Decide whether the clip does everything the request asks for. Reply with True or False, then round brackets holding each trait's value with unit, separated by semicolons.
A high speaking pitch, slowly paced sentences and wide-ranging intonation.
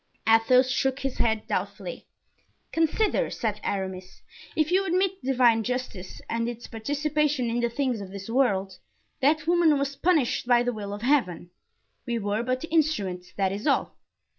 False (245 Hz; 165 wpm; 5.7 semitones)